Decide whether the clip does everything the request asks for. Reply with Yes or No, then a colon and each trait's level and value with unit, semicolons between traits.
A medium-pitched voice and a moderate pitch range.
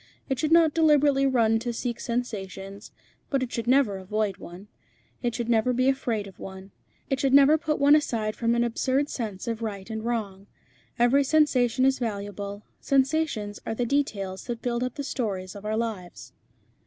No: high, 235 Hz; average, 4.6 semitones